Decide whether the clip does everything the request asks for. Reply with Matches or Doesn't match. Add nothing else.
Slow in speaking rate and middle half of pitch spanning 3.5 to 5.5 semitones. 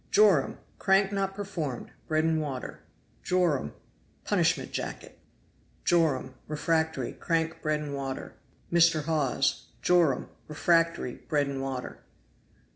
Matches